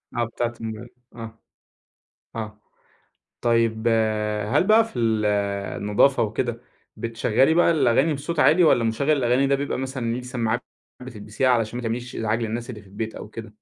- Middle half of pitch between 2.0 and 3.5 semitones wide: Yes, average, 2.9 semitones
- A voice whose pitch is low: Yes, low, 120 Hz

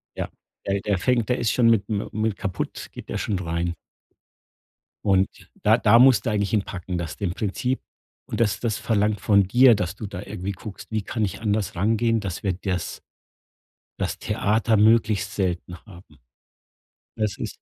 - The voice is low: Yes, low, 105 Hz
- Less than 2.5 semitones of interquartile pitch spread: No, average, 2.8 semitones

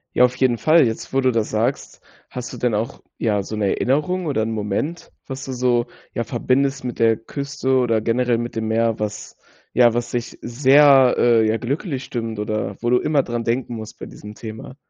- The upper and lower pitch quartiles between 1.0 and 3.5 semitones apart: Yes, average, 2.9 semitones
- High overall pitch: No, low, 120 Hz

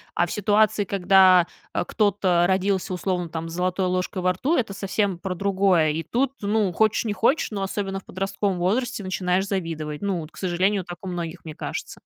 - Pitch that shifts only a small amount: Yes, narrow, 2.3 semitones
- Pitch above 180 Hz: Yes, high, 190 Hz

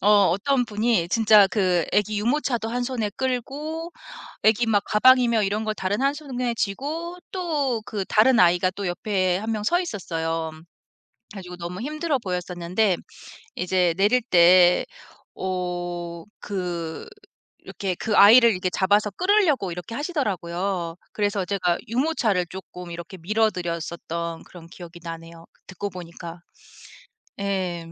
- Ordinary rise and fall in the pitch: Yes, average, 5.0 semitones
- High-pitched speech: Yes, high, 200 Hz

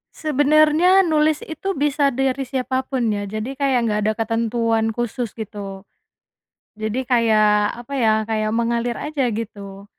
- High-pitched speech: Yes, high, 240 Hz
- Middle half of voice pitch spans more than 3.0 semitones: Yes, average, 4.2 semitones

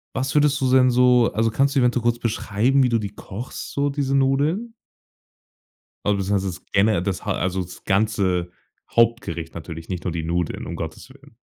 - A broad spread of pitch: Yes, wide, 6.0 semitones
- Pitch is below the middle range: Yes, low, 115 Hz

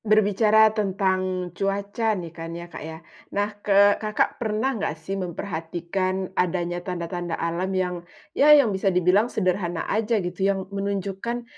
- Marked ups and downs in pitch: No, average, 2.9 semitones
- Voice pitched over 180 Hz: Yes, high, 190 Hz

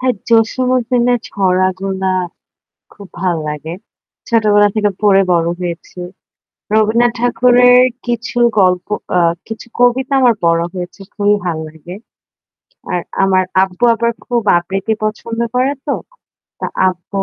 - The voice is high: Yes, high, 205 Hz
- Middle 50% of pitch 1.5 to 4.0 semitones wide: No, average, 4.7 semitones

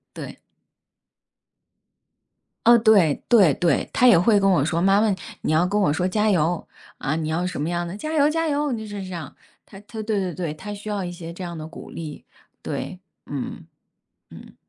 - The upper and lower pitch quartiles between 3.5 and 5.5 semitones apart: Yes, average, 4.1 semitones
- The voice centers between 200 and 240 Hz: No, medium, 185 Hz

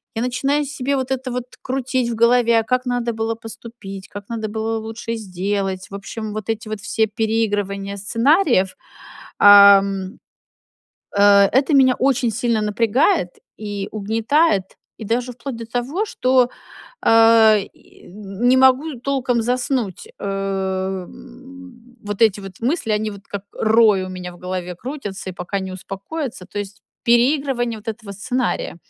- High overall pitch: Yes, high, 225 Hz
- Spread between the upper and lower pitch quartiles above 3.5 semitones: Yes, average, 3.9 semitones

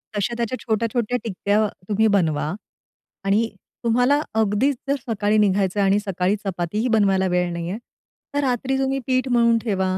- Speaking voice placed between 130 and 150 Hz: No, high, 210 Hz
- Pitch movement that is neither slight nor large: Yes, average, 3.5 semitones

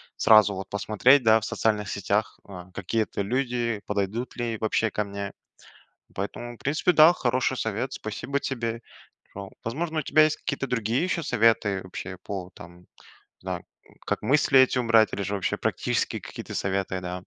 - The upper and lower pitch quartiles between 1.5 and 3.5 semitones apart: No, average, 4.1 semitones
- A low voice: Yes, low, 110 Hz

